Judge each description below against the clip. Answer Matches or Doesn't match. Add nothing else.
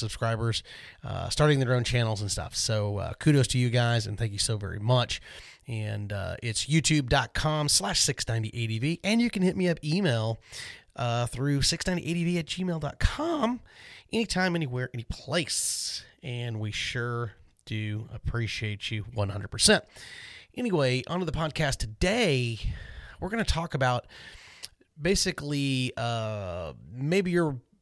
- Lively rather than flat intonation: Matches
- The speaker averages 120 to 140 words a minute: Matches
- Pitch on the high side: Doesn't match